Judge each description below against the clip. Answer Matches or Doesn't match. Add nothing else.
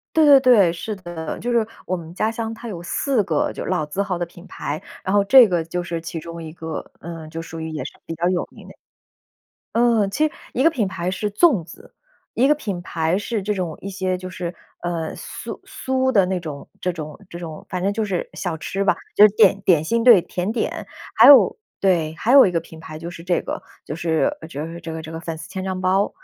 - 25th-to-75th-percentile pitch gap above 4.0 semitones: Matches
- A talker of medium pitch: Matches